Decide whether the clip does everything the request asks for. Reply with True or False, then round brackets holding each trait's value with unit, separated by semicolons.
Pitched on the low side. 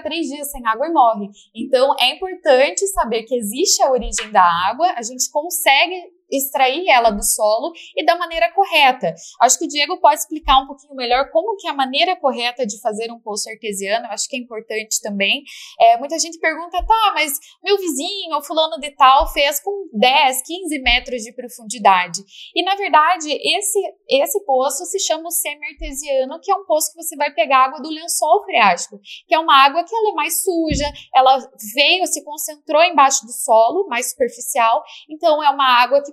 False (290 Hz)